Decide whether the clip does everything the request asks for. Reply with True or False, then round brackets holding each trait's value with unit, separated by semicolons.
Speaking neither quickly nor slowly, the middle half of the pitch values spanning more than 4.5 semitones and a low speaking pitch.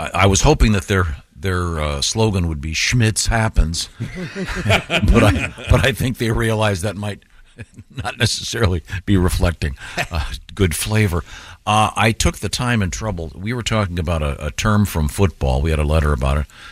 True (180 wpm; 5.3 semitones; 95 Hz)